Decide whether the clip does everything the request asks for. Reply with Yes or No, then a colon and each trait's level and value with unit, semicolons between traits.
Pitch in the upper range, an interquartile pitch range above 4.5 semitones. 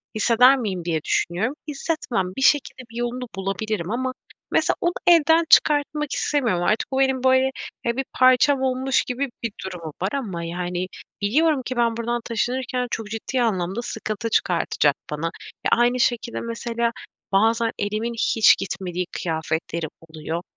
Yes: high, 230 Hz; wide, 5.4 semitones